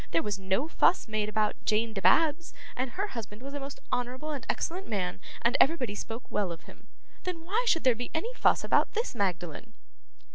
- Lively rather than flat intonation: Yes, wide, 7.4 semitones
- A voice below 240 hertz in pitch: No, high, 245 Hz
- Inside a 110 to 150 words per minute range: No, average, 195 wpm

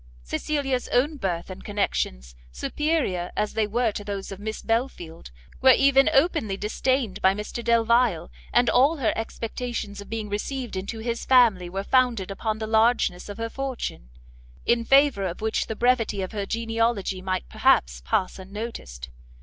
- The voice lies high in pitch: Yes, high, 220 Hz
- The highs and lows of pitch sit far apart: No, average, 4.2 semitones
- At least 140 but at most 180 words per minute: Yes, average, 160 wpm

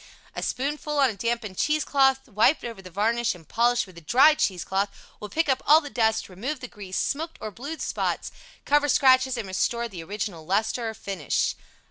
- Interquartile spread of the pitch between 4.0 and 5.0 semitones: No, wide, 5.6 semitones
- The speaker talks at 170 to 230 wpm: Yes, average, 200 wpm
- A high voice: Yes, high, 235 Hz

